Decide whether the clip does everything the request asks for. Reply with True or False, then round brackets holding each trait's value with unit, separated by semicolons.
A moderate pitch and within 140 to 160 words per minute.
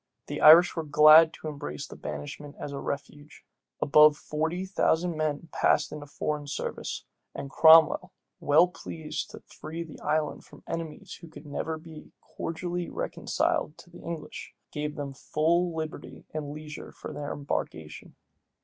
True (155 Hz; 150 wpm)